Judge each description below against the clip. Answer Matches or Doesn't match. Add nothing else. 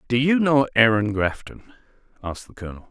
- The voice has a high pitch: Doesn't match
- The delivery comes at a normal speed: Matches